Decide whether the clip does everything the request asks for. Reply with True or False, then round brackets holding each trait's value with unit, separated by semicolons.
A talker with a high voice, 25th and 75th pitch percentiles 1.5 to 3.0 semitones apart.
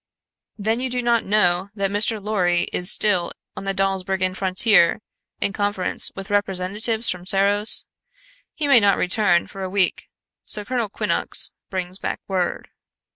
True (195 Hz; 2.4 semitones)